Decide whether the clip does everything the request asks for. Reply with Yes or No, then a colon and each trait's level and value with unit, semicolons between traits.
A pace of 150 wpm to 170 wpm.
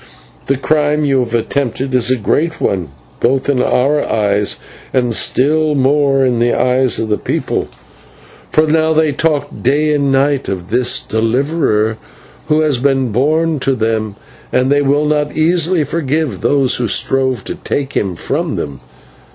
Yes: average, 160 wpm